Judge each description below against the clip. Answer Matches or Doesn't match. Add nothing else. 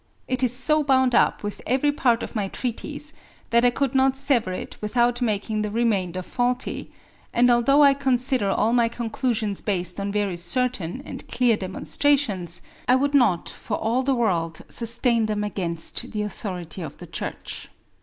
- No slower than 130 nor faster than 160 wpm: Doesn't match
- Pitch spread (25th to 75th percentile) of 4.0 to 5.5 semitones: Matches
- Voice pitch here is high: Matches